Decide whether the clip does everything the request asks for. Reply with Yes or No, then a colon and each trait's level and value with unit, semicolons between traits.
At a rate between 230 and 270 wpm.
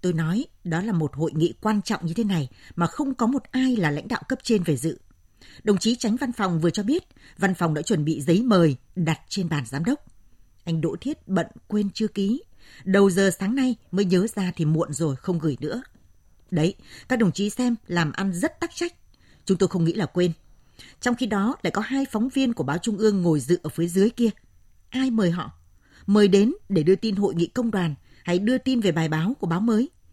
Yes: average, 235 wpm